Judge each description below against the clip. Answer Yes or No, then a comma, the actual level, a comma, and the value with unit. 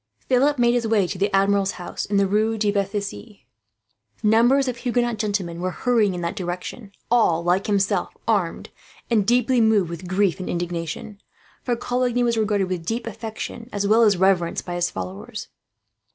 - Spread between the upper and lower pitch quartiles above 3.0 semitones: Yes, average, 3.9 semitones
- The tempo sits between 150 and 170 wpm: No, average, 180 wpm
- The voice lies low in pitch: No, high, 205 Hz